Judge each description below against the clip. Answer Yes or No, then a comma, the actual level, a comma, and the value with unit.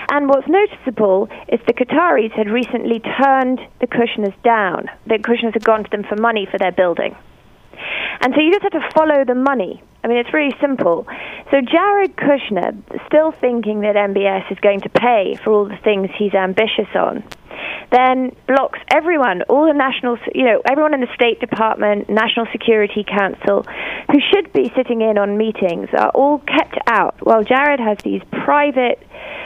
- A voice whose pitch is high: Yes, high, 240 Hz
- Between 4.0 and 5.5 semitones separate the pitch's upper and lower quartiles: Yes, average, 4.8 semitones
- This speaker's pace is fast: No, average, 175 wpm